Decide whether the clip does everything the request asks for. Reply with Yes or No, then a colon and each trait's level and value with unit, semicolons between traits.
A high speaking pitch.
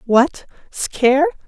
Yes: very high, 255 Hz